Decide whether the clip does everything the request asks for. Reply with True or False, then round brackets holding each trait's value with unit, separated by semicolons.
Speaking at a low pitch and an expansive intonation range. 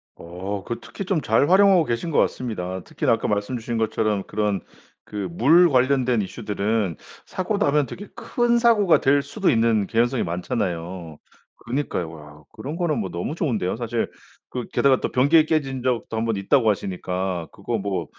True (115 Hz; 6.6 semitones)